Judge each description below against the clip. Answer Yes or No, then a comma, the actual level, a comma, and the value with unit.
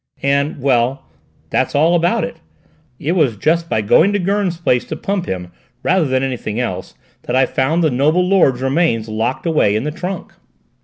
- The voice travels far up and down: Yes, wide, 5.7 semitones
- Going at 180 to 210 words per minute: Yes, average, 185 wpm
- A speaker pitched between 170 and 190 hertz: No, medium, 140 Hz